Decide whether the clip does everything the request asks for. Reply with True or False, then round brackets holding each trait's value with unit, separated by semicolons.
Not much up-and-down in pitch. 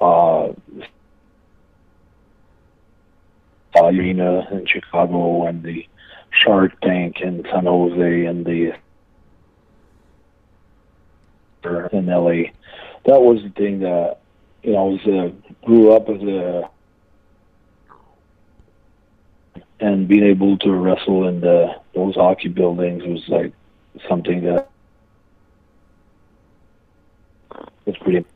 True (2.3 semitones)